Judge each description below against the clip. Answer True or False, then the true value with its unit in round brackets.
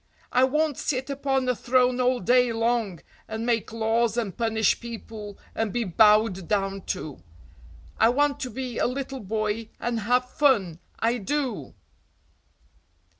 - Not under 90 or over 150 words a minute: True (145 wpm)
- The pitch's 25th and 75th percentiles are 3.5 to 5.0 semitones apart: False (2.9 semitones)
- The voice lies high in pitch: True (235 Hz)